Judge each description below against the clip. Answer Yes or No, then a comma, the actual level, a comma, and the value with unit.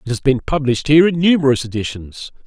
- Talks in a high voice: No, low, 135 Hz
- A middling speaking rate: Yes, average, 195 wpm